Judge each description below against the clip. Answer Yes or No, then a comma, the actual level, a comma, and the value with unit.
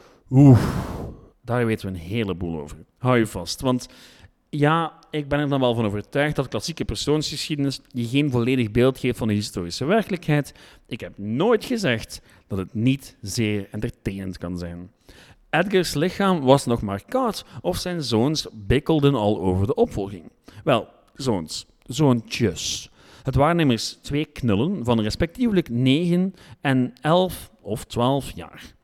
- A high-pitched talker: No, low, 125 Hz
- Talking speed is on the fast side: No, average, 150 wpm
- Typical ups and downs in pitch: No, wide, 5.8 semitones